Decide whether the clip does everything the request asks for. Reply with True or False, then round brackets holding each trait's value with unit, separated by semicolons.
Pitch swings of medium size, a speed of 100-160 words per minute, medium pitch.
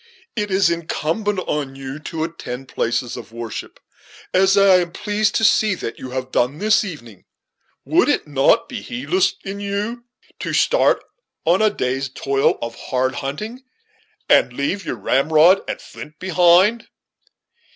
False (7.3 semitones; 155 wpm; 170 Hz)